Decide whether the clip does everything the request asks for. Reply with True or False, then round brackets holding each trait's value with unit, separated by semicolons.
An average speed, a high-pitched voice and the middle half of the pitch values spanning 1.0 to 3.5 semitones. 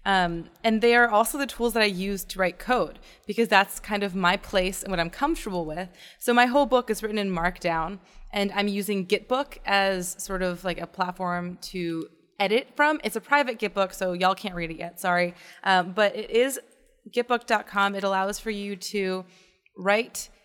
True (195 wpm; 200 Hz; 3.2 semitones)